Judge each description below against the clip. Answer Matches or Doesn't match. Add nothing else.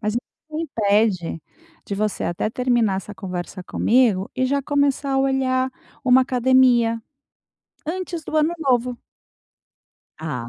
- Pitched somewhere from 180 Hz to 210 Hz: Doesn't match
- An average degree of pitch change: Matches